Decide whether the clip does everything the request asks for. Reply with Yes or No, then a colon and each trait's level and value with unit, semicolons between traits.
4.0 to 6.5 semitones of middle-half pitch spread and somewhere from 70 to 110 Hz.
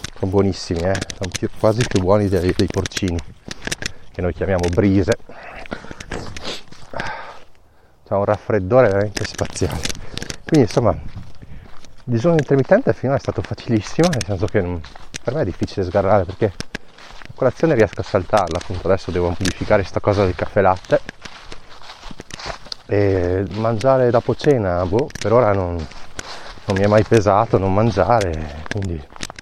No: average, 3.5 semitones; low, 100 Hz